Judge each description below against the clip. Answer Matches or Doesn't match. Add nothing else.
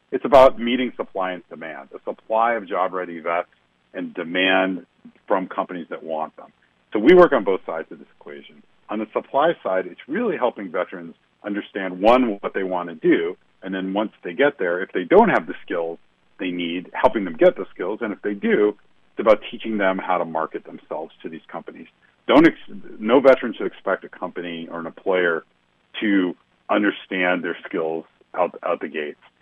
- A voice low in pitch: Matches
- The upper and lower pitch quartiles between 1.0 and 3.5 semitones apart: Doesn't match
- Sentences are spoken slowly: Doesn't match